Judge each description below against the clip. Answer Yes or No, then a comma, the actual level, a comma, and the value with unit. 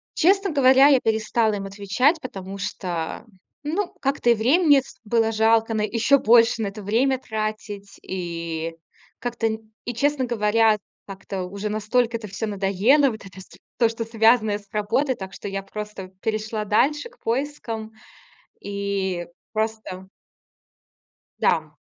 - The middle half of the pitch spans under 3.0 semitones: No, average, 3.4 semitones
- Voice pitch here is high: Yes, high, 220 Hz